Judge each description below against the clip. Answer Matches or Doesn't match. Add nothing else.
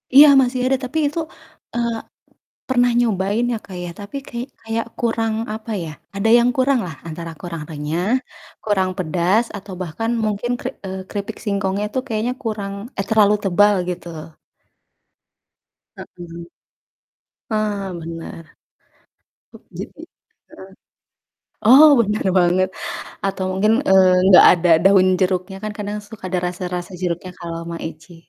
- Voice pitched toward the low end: Doesn't match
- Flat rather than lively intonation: Doesn't match